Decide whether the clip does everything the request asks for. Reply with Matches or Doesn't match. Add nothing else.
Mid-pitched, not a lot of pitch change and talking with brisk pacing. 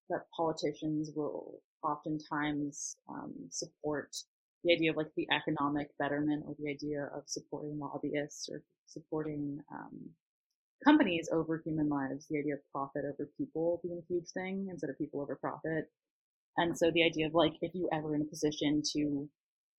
Doesn't match